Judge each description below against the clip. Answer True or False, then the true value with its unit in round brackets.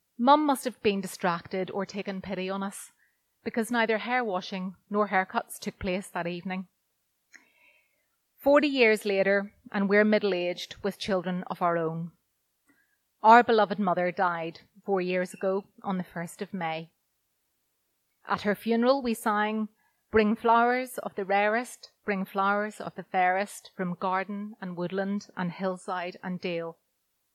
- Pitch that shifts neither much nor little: True (3.0 semitones)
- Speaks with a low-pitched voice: False (200 Hz)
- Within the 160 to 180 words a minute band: False (145 wpm)